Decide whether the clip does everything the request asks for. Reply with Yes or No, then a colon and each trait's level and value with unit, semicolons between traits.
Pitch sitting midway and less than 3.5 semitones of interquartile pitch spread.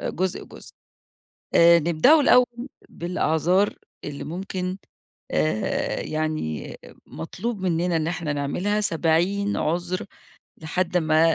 Yes: medium, 170 Hz; average, 3.1 semitones